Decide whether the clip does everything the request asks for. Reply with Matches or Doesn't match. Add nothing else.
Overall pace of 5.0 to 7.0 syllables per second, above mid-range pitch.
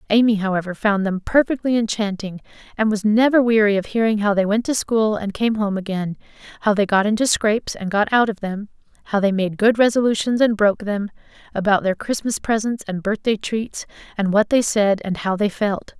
Matches